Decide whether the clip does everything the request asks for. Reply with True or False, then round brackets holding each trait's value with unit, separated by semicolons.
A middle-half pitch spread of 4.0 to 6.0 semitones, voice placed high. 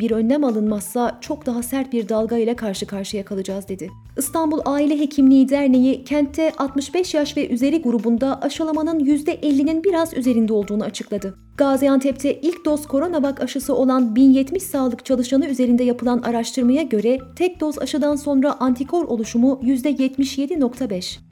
False (3.5 semitones; 265 Hz)